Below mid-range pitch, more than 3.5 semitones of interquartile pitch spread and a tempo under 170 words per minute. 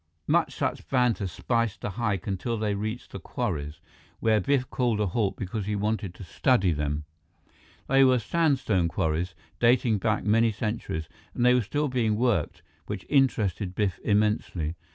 Yes: low, 105 Hz; average, 4.2 semitones; average, 160 wpm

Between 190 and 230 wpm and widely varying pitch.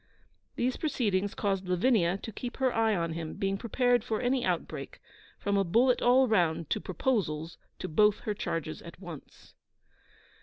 No: average, 160 wpm; wide, 6.1 semitones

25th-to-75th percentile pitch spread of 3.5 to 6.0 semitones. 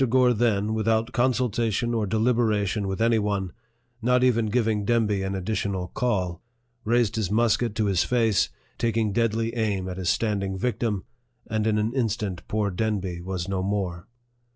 No: average, 2.9 semitones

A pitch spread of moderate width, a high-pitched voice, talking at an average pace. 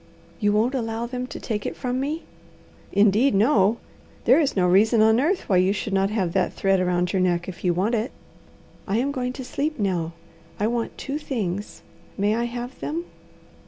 Yes: average, 4.6 semitones; high, 220 Hz; average, 195 wpm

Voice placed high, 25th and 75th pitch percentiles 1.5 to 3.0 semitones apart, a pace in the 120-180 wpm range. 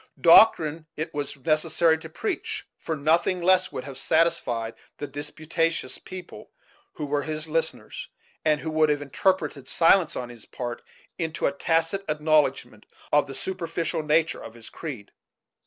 No: medium, 155 Hz; average, 2.7 semitones; average, 150 wpm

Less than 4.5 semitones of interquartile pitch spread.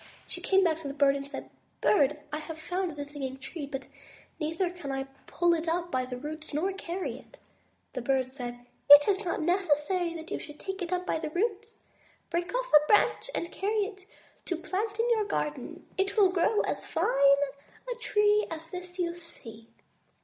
No: average, 4.8 semitones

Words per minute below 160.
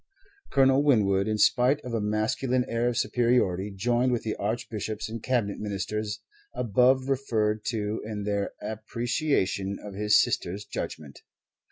Yes: average, 140 wpm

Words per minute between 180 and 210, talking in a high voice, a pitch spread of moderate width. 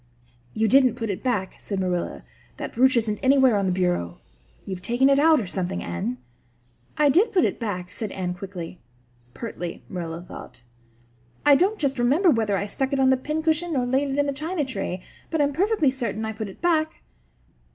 No: average, 195 wpm; high, 245 Hz; wide, 7.1 semitones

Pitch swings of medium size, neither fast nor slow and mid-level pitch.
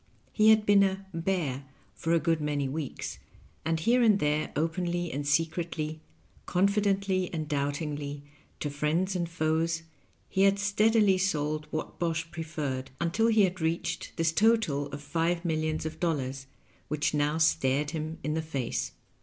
Yes: average, 3.8 semitones; average, 155 wpm; medium, 160 Hz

